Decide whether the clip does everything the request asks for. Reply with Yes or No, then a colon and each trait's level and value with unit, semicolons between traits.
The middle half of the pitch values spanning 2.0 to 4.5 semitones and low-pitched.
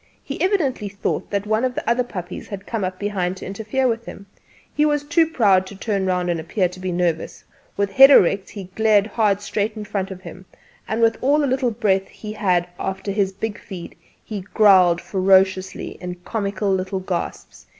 No: average, 3.0 semitones; high, 200 Hz